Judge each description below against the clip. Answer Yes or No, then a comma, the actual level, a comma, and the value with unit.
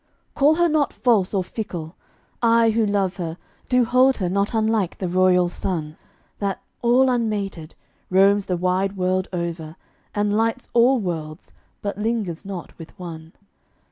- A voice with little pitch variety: No, average, 4.3 semitones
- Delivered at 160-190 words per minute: No, average, 150 wpm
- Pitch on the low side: No, high, 195 Hz